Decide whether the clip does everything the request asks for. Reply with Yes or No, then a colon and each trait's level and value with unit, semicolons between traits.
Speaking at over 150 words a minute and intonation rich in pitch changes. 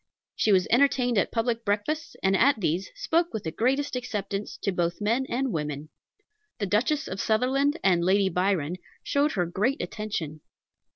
Yes: average, 165 wpm; wide, 5.9 semitones